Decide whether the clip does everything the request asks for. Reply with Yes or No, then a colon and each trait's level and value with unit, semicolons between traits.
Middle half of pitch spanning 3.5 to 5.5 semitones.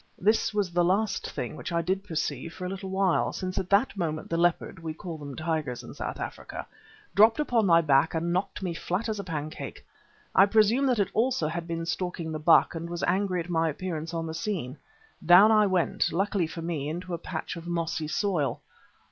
No: average, 3.1 semitones